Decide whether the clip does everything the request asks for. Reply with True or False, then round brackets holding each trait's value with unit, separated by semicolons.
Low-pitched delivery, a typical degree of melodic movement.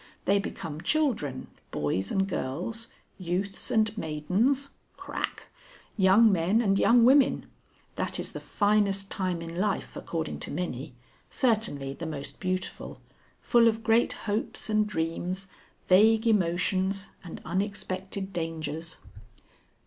False (190 Hz; 4.5 semitones)